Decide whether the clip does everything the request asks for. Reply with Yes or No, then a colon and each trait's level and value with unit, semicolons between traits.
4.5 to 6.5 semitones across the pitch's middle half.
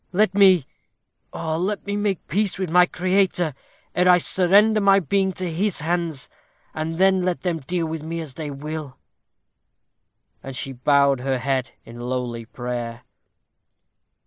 Yes: wide, 5.5 semitones